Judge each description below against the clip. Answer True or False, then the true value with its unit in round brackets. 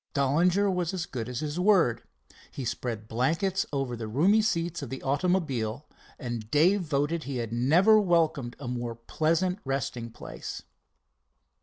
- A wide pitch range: True (6.3 semitones)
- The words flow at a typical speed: True (150 wpm)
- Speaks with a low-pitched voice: False (145 Hz)